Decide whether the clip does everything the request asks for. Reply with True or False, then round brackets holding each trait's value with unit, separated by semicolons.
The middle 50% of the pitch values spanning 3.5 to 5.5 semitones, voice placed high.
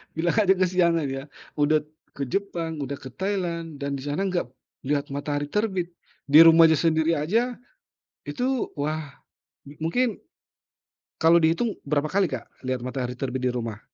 False (4.4 semitones; 160 Hz)